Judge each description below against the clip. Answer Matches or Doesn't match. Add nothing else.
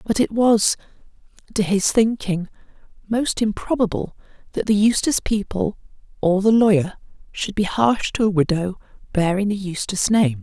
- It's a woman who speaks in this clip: Matches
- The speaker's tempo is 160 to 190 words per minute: Doesn't match